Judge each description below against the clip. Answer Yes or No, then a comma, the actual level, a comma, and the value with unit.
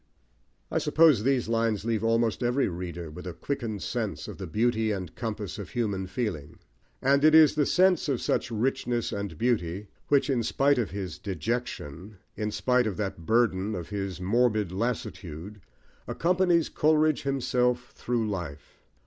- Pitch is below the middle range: Yes, low, 115 Hz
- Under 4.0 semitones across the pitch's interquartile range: No, average, 4.5 semitones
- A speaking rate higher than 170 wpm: No, average, 155 wpm